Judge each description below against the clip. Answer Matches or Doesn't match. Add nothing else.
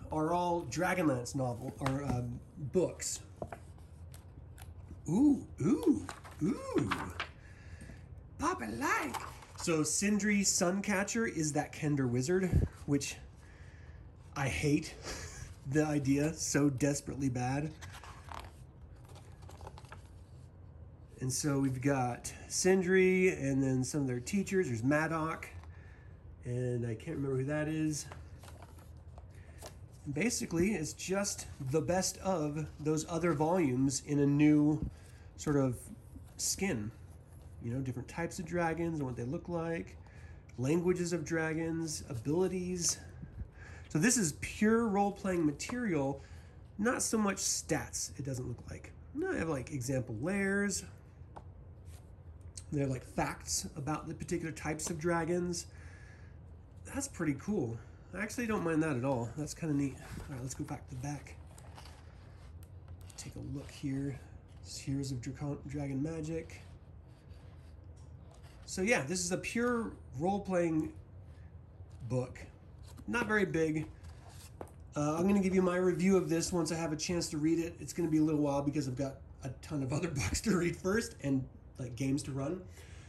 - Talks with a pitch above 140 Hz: Doesn't match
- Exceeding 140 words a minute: Doesn't match